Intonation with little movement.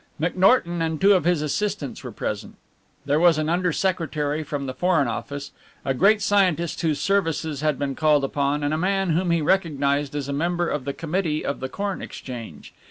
No: average, 3.9 semitones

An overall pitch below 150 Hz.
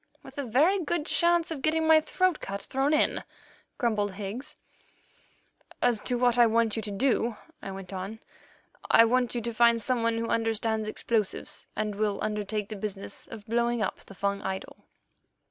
No: high, 230 Hz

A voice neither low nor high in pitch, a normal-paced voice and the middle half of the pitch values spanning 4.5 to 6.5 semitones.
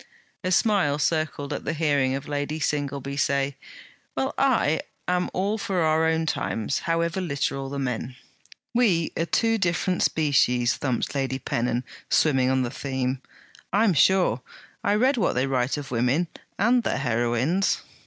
Yes: medium, 145 Hz; average, 155 wpm; average, 5.0 semitones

